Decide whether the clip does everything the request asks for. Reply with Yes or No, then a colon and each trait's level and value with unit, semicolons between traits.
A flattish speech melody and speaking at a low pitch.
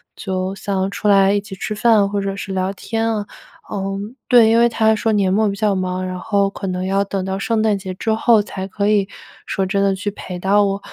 No: narrow, 1.8 semitones; high, 200 Hz